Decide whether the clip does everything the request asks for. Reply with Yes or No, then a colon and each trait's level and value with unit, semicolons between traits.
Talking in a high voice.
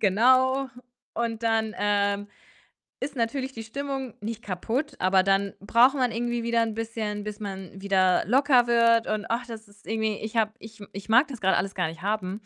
Yes: high, 220 Hz